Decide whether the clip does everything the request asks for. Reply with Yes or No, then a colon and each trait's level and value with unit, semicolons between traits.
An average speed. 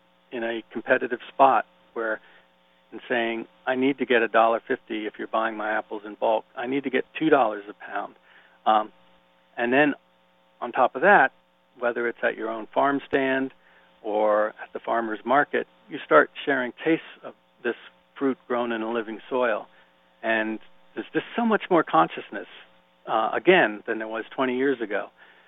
Yes: average, 175 wpm